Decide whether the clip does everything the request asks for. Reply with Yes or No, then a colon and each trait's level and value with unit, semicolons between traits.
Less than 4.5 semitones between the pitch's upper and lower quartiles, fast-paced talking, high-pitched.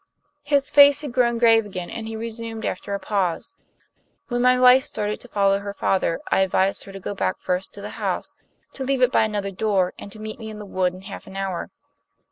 Yes: average, 3.5 semitones; fast, 230 wpm; high, 210 Hz